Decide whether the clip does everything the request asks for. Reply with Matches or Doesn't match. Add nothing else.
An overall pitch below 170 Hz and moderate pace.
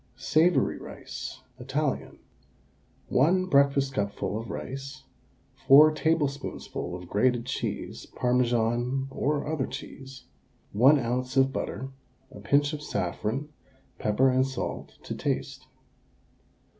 Doesn't match